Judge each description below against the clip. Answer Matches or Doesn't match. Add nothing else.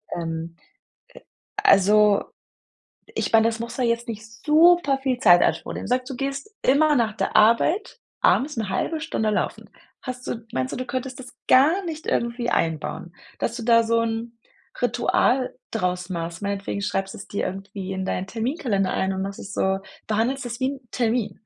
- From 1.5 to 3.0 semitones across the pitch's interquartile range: Doesn't match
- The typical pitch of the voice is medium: Doesn't match